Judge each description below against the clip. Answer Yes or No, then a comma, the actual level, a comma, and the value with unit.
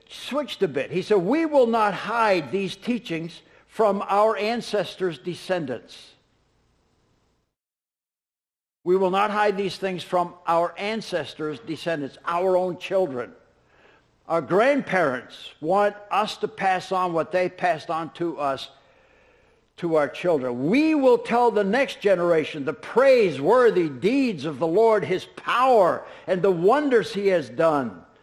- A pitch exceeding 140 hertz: Yes, medium, 185 Hz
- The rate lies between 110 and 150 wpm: Yes, slow, 135 wpm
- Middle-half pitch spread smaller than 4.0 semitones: No, average, 5.2 semitones